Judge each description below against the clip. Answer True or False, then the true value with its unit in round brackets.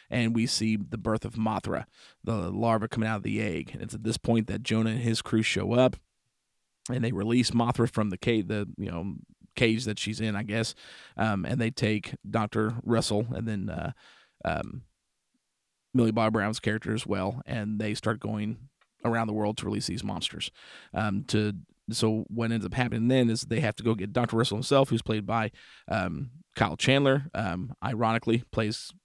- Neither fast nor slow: True (195 wpm)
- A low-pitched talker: True (110 Hz)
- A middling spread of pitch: False (1.5 semitones)